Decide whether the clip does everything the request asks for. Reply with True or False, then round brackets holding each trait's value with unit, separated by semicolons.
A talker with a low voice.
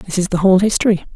False (190 Hz)